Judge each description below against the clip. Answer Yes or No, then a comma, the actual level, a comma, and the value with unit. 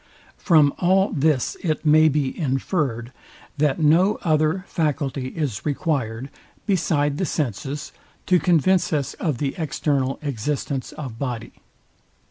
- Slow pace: Yes, slow, 120 wpm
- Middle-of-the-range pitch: Yes, medium, 150 Hz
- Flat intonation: No, average, 3.1 semitones